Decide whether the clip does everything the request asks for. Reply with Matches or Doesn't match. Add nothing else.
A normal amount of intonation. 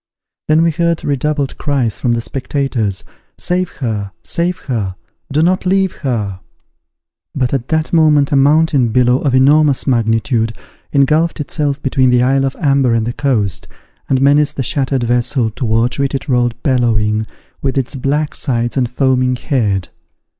Matches